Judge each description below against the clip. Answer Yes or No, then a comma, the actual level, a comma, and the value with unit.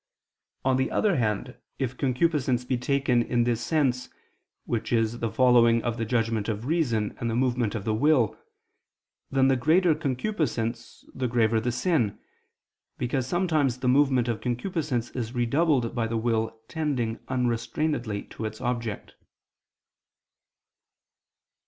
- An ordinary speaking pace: No, slow, 125 wpm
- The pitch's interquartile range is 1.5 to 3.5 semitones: Yes, average, 2.9 semitones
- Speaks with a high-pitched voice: No, low, 125 Hz